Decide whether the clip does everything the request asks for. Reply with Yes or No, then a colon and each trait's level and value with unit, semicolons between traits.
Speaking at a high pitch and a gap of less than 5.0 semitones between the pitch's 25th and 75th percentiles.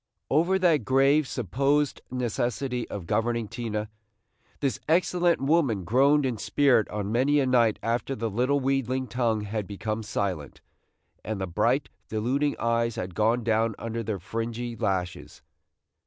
No: low, 120 Hz; average, 4.0 semitones